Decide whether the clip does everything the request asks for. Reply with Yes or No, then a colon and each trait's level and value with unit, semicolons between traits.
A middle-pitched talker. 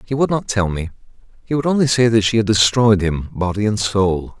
No: low, 110 Hz